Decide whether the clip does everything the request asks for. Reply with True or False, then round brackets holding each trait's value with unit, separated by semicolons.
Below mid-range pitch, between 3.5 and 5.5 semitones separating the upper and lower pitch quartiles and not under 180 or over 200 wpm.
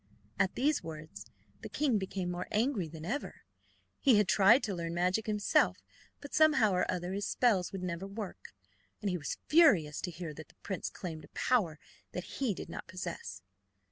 False (190 Hz; 4.5 semitones; 185 wpm)